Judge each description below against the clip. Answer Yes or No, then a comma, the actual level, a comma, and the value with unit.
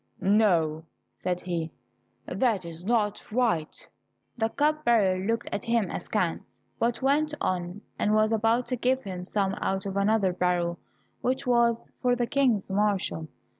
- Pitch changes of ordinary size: Yes, average, 4.6 semitones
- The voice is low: No, high, 210 Hz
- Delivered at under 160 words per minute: Yes, average, 150 wpm